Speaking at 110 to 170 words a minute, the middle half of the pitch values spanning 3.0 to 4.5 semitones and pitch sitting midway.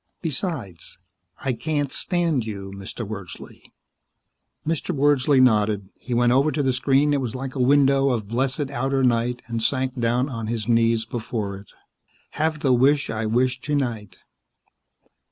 No: average, 155 wpm; average, 3.5 semitones; low, 125 Hz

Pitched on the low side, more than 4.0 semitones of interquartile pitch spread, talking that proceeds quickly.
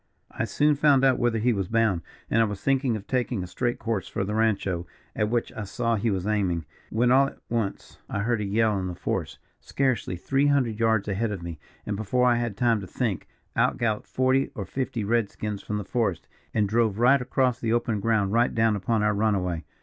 No: low, 110 Hz; average, 3.2 semitones; fast, 225 wpm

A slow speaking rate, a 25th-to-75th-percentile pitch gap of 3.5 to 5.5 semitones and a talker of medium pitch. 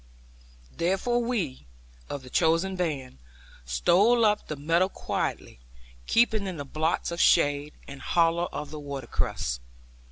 Yes: slow, 130 wpm; average, 5.1 semitones; medium, 165 Hz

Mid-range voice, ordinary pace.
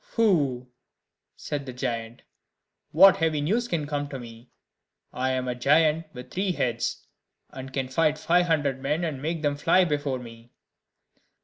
Yes: medium, 145 Hz; average, 155 wpm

